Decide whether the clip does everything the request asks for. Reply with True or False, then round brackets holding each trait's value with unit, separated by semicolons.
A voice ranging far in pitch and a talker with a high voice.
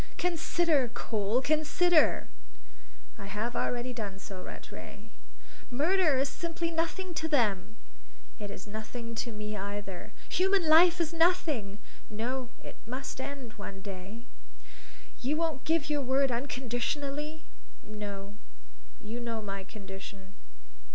True (7.0 semitones; 245 Hz)